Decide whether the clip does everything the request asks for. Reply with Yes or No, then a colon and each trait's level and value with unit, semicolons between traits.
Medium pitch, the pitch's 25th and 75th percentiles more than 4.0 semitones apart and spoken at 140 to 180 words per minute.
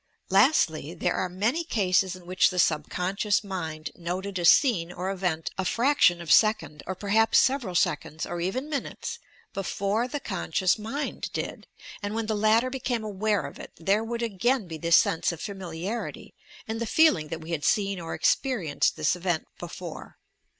No: high, 195 Hz; average, 4.5 semitones; average, 170 wpm